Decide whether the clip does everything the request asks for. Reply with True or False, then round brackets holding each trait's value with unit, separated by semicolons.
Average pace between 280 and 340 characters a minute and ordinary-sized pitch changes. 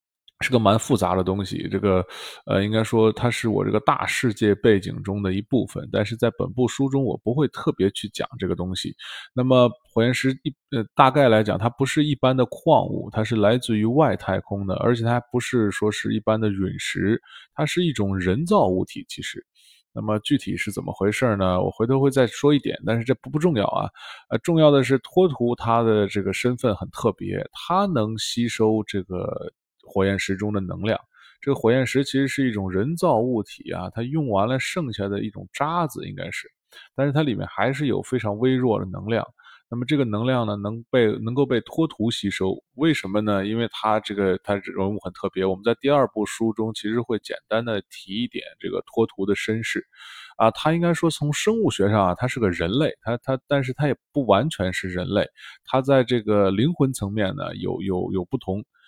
True (300 characters per minute; 4.6 semitones)